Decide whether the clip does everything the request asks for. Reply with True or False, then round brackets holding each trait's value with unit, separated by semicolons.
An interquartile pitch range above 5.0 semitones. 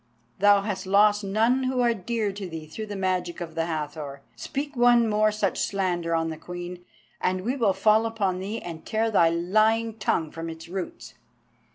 False (4.3 semitones)